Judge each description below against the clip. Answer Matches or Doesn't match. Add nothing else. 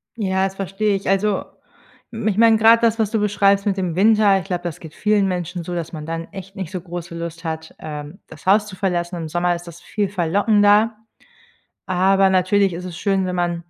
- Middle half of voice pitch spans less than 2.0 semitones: Doesn't match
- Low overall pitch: Doesn't match